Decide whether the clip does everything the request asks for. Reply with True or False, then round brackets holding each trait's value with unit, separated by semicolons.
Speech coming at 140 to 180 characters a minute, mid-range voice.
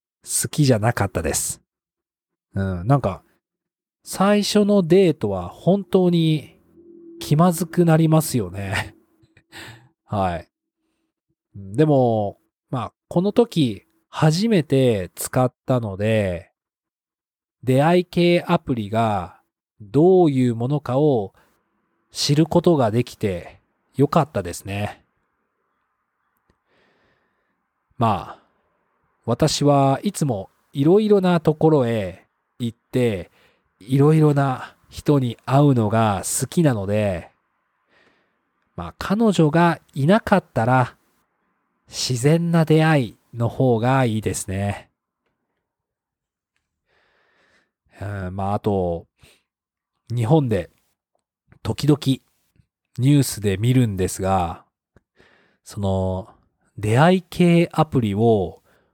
False (175 characters per minute; 130 Hz)